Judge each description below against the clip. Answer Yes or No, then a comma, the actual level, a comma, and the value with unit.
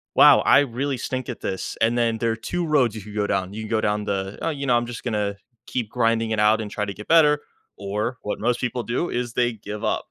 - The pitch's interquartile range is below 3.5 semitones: Yes, average, 2.8 semitones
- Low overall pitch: Yes, low, 115 Hz